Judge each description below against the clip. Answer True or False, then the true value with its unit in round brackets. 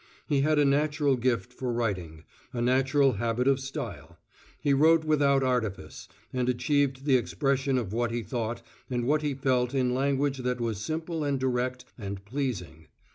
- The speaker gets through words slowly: False (170 wpm)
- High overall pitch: False (130 Hz)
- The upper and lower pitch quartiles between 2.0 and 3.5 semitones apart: True (2.9 semitones)